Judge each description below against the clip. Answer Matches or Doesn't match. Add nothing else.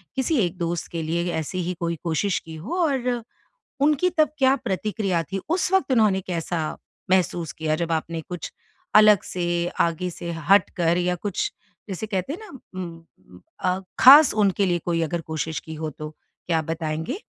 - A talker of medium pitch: Matches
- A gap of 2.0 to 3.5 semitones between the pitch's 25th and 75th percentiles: Doesn't match